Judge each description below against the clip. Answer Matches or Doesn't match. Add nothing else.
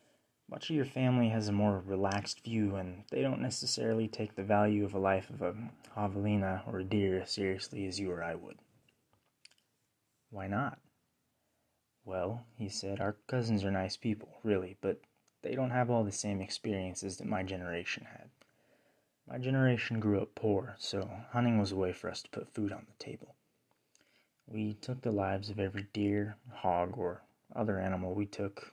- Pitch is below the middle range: Matches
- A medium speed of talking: Matches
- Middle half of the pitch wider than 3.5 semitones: Doesn't match